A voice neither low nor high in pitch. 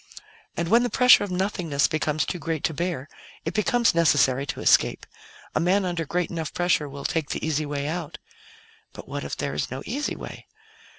Yes: medium, 165 Hz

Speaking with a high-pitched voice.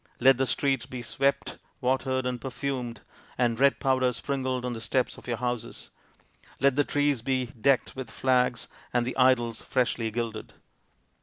No: low, 125 Hz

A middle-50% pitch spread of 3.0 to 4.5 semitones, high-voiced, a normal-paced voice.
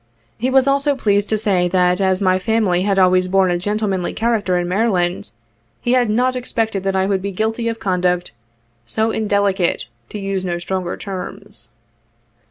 Yes: average, 3.4 semitones; high, 195 Hz; average, 180 wpm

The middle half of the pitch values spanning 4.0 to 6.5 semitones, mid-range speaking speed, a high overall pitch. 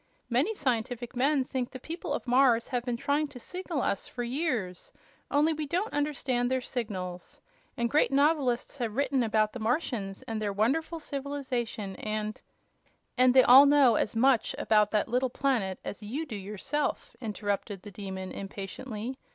Yes: average, 4.7 semitones; average, 170 wpm; high, 245 Hz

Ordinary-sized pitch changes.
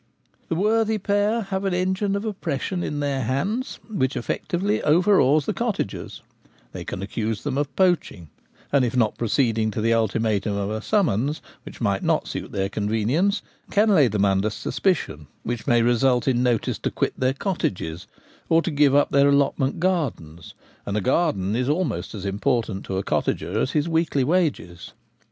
No: wide, 8.5 semitones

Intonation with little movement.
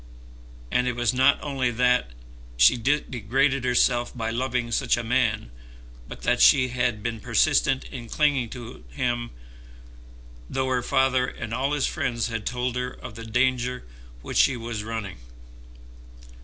Yes: narrow, 2.1 semitones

